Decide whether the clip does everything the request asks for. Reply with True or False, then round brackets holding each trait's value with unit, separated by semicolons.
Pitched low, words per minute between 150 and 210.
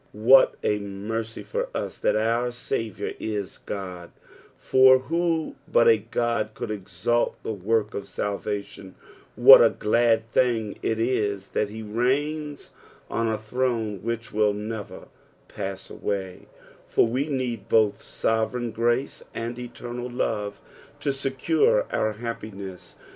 False (115 Hz; 135 wpm)